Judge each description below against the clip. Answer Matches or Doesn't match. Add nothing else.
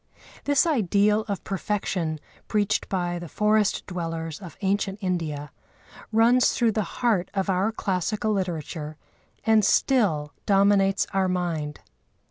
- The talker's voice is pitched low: Doesn't match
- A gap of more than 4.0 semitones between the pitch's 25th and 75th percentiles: Doesn't match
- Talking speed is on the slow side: Matches